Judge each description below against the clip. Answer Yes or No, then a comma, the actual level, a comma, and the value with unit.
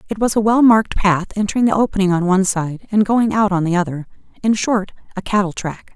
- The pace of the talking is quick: Yes, fast, 230 wpm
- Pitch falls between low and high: No, high, 200 Hz